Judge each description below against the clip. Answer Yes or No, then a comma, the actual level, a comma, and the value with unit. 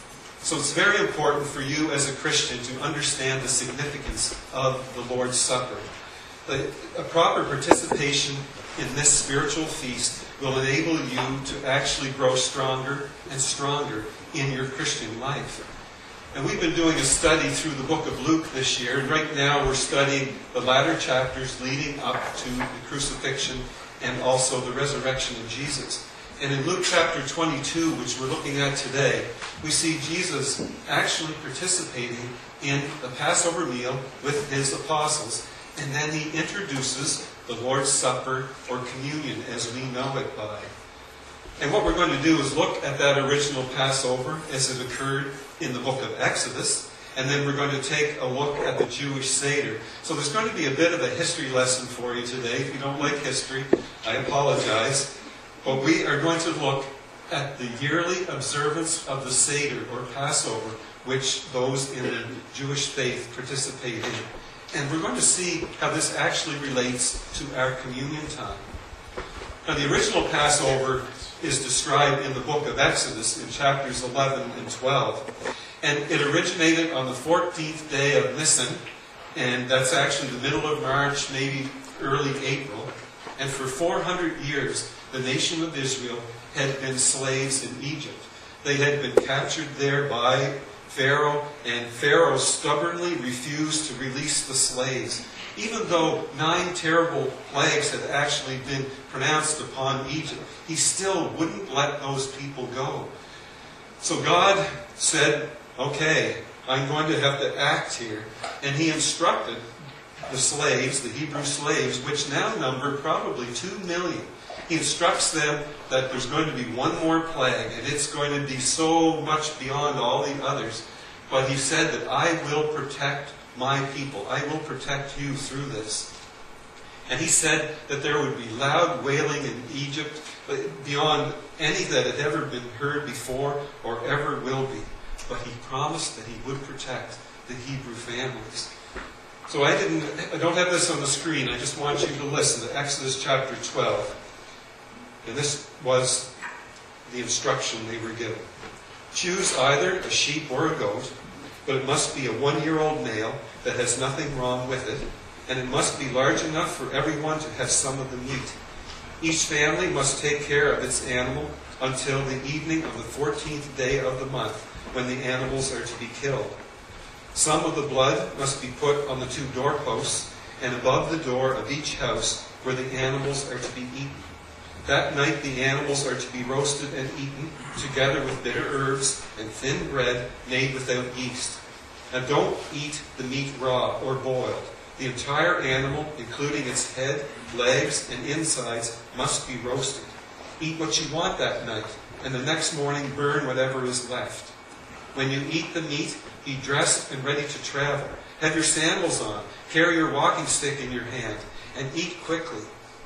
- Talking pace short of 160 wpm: No, average, 165 wpm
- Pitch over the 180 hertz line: No, medium, 140 Hz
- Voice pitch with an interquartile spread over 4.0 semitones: No, average, 2.7 semitones